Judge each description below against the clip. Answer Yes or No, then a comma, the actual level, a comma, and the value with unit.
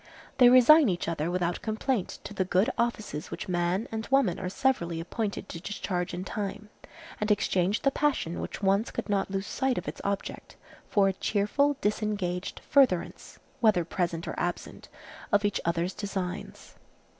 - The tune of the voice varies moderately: Yes, average, 3.8 semitones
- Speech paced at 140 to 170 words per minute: Yes, average, 165 wpm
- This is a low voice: No, high, 200 Hz